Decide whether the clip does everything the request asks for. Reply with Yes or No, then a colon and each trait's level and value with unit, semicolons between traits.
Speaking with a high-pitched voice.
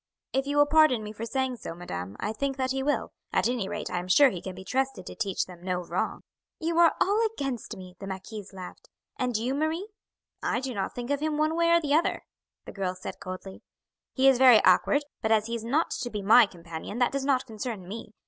Yes: high, 240 Hz